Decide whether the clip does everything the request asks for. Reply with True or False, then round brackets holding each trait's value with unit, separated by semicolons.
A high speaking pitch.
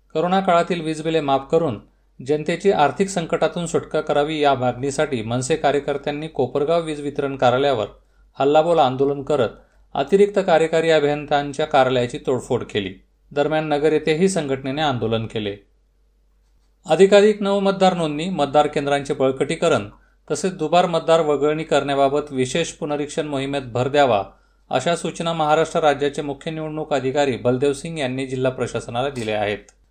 False (150 Hz)